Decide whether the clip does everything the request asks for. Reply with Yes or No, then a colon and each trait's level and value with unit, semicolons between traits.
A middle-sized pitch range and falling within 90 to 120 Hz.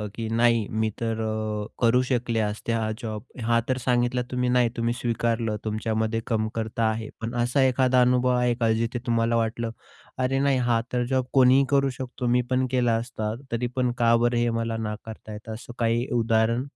No: narrow, 1.8 semitones; low, 115 Hz